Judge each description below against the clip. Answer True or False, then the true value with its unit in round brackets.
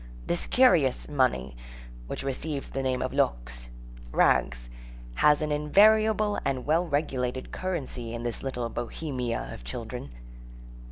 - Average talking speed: False (115 wpm)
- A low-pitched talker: True (130 Hz)